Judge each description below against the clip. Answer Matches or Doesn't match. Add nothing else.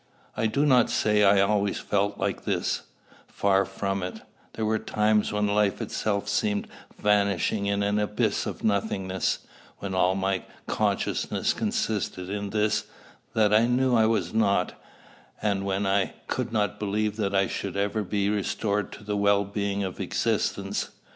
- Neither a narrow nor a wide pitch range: Doesn't match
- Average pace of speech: Matches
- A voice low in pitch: Matches